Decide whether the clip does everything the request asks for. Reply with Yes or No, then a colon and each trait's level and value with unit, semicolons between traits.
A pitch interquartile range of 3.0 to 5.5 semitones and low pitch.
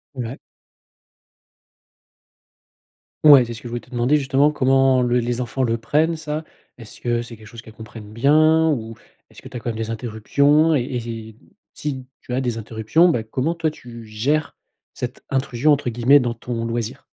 Yes: average, 3.8 semitones; low, 125 Hz